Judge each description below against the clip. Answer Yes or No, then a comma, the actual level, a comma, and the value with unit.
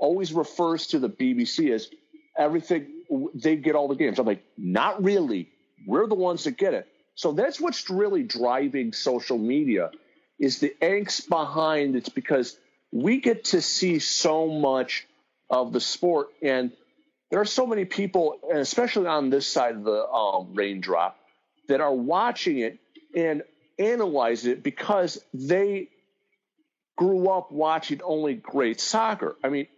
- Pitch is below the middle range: No, medium, 180 Hz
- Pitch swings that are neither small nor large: No, wide, 8.2 semitones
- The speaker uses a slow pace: No, average, 155 wpm